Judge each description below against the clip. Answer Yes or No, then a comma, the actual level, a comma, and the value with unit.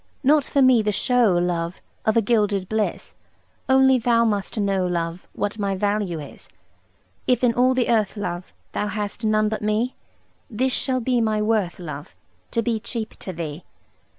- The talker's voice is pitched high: Yes, high, 215 Hz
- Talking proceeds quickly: No, average, 175 wpm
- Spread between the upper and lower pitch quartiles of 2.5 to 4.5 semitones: Yes, average, 3.8 semitones